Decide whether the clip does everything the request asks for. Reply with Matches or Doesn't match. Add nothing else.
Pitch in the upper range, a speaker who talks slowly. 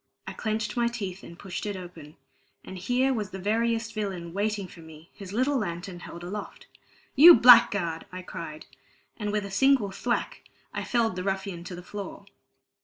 Doesn't match